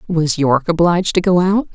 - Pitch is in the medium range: Yes, medium, 175 Hz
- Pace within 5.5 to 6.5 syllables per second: Yes, 5.8 syllables/s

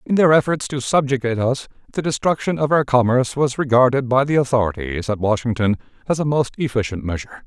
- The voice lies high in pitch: No, low, 125 Hz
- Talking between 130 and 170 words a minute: No, average, 185 wpm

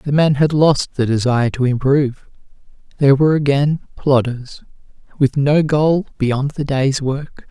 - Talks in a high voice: No, medium, 140 Hz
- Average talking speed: Yes, average, 150 wpm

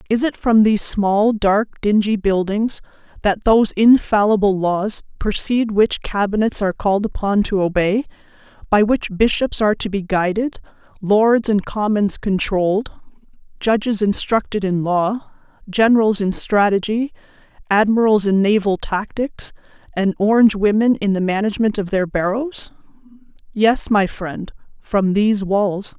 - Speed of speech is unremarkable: No, slow, 130 wpm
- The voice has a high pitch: Yes, high, 205 Hz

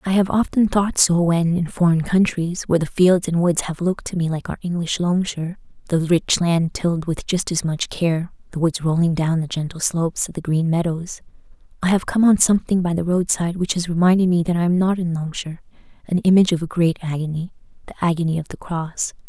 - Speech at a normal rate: No, fast, 210 wpm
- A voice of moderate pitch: Yes, medium, 170 Hz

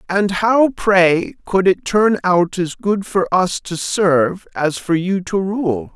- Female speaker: No, male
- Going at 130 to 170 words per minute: No, average, 180 wpm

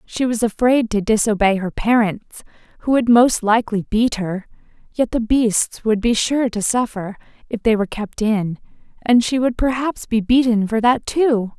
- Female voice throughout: Yes, female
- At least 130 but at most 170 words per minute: No, average, 180 wpm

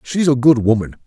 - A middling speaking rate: No, fast, 225 wpm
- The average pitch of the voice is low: Yes, low, 130 Hz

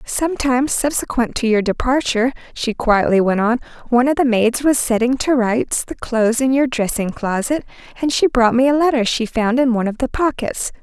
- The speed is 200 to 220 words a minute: Yes, fast, 205 wpm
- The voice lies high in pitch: Yes, high, 245 Hz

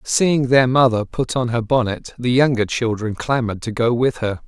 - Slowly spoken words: No, average, 200 wpm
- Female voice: No, male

